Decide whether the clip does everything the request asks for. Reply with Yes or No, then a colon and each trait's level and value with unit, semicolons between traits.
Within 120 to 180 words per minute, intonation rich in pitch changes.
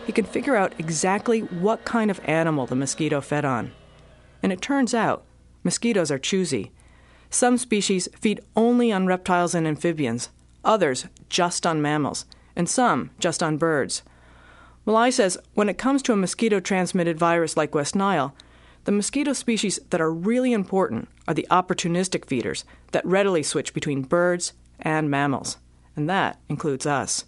Yes: average, 160 wpm; wide, 6.4 semitones